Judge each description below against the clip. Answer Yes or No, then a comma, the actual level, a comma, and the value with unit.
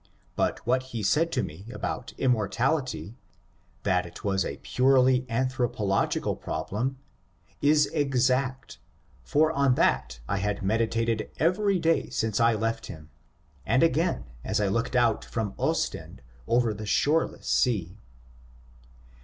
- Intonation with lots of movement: No, average, 4.7 semitones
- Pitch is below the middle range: Yes, low, 115 Hz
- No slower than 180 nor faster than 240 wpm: No, average, 140 wpm